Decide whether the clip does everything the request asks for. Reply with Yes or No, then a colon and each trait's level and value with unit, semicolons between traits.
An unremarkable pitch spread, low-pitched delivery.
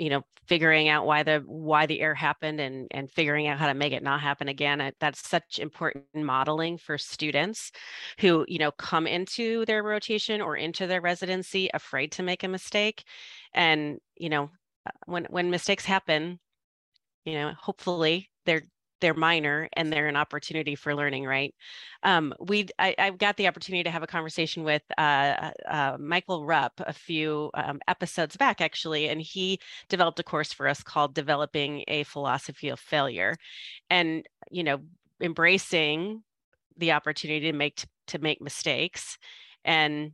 No: average, 3.1 semitones; medium, 160 Hz